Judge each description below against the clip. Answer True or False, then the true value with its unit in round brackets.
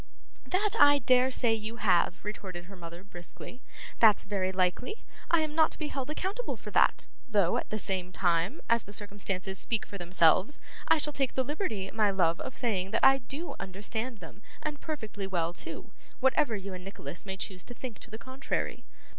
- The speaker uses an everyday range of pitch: False (5.9 semitones)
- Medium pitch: False (210 Hz)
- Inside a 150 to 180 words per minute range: False (195 wpm)